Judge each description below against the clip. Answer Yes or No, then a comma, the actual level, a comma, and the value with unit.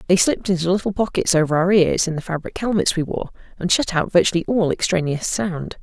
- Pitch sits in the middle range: Yes, medium, 180 Hz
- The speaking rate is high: Yes, fast, 215 wpm